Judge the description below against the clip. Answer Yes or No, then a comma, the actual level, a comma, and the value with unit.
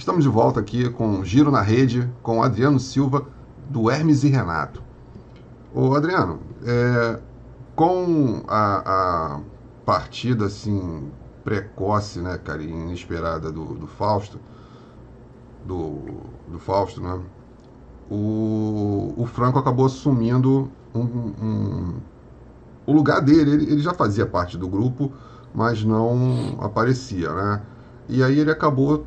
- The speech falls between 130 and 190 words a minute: No, slow, 120 wpm